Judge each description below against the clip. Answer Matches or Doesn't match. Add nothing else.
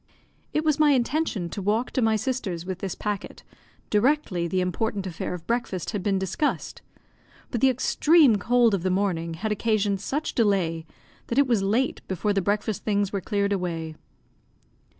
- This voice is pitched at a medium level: Doesn't match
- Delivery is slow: Doesn't match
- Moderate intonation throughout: Matches